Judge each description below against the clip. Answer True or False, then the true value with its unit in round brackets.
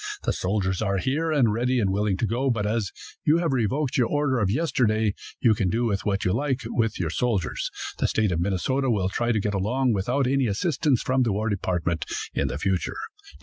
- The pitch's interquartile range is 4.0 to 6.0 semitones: True (4.8 semitones)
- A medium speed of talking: False (210 wpm)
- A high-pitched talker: False (110 Hz)